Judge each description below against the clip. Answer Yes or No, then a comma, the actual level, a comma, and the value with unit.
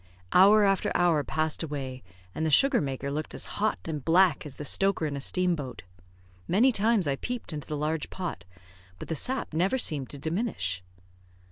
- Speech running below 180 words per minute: No, average, 190 wpm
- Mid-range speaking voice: Yes, medium, 160 Hz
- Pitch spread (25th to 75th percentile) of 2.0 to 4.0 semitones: No, average, 5.3 semitones